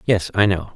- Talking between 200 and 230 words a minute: No, fast, 240 wpm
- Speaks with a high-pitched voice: No, very low, 95 Hz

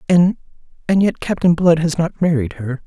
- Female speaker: No, male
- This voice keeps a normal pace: Yes, average, 190 wpm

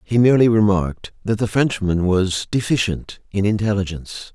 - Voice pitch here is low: Yes, low, 100 Hz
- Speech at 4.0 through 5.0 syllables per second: No, 5.5 syllables/s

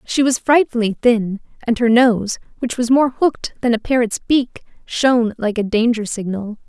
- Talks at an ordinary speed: Yes, average, 180 wpm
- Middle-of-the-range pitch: No, high, 235 Hz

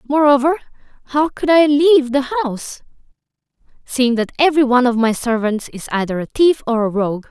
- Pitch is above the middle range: Yes, very high, 260 Hz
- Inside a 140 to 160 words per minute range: No, average, 170 wpm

